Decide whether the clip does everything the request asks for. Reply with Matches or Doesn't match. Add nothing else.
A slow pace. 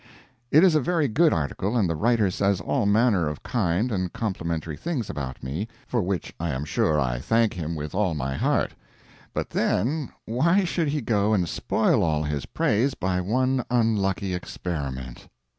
Doesn't match